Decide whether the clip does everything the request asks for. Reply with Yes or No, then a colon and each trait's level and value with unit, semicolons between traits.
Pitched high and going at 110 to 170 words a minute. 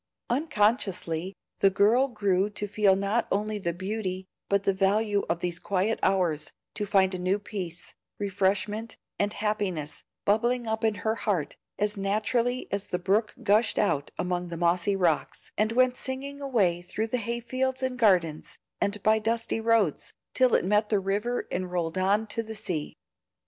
Yes: high, 205 Hz; average, 165 wpm